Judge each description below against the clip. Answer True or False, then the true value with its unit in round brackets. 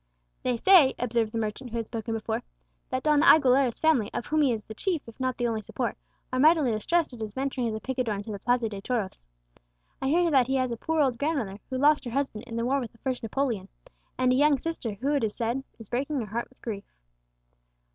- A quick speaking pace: True (240 wpm)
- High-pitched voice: True (250 Hz)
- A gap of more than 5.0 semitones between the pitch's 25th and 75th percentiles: False (3.7 semitones)